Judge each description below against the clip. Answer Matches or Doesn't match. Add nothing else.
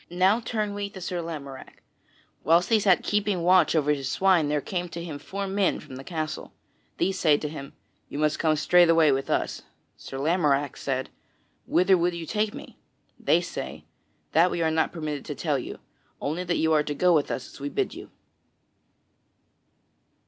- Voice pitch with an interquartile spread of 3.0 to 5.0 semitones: Matches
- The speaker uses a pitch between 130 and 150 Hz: Doesn't match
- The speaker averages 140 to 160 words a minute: Doesn't match